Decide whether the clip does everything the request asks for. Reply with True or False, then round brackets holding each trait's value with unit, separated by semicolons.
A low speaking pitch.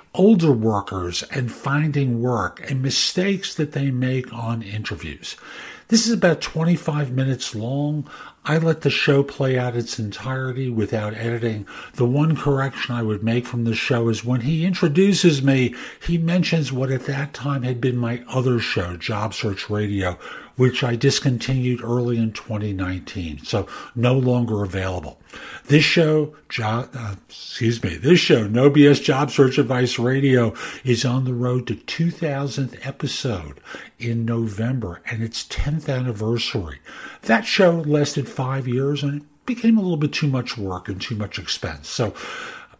True (125 Hz)